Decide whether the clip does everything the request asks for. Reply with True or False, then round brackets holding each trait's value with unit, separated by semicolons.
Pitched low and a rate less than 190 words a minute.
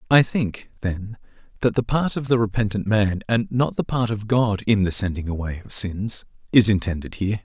False (105 Hz; 200 wpm)